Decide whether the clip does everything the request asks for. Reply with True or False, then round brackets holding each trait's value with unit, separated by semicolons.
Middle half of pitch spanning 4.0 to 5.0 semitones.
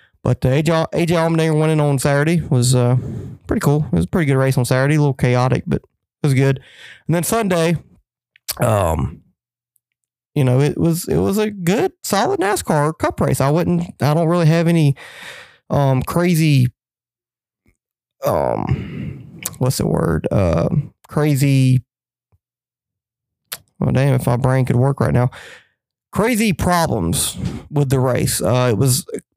True (4.6 semitones)